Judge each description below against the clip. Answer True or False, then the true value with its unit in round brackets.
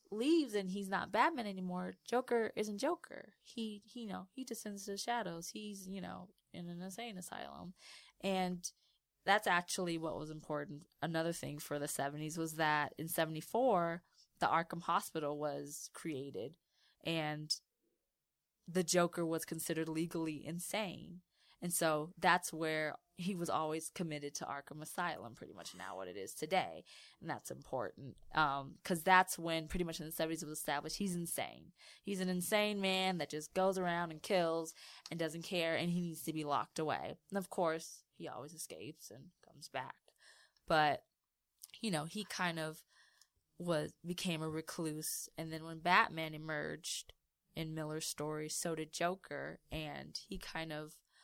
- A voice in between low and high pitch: True (170 Hz)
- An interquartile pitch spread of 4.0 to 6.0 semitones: False (3.2 semitones)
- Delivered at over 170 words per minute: False (165 wpm)